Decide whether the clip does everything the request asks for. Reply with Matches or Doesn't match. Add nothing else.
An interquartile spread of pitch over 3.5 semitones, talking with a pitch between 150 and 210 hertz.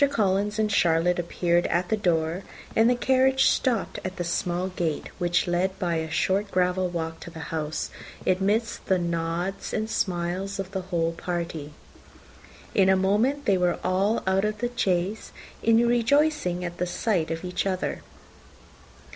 Doesn't match